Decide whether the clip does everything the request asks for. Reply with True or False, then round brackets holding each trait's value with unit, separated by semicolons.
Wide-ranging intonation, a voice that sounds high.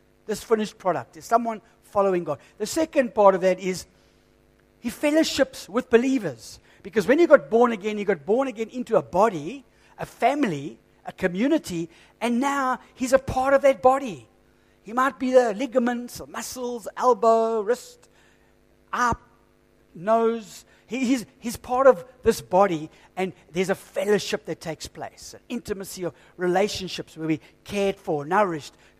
True (6.0 semitones; 220 Hz)